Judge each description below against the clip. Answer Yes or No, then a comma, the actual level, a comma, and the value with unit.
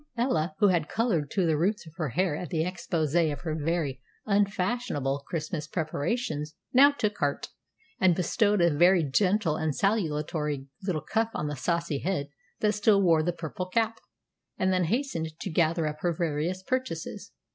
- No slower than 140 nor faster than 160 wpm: No, average, 170 wpm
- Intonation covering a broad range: No, average, 4.4 semitones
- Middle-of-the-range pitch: Yes, medium, 170 Hz